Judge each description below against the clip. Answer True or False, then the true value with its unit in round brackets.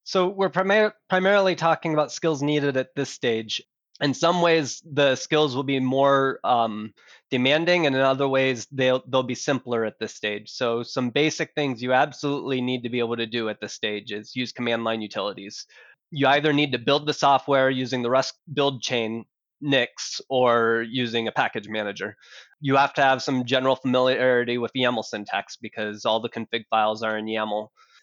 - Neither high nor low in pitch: False (130 Hz)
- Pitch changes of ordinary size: True (3.7 semitones)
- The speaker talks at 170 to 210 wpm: True (190 wpm)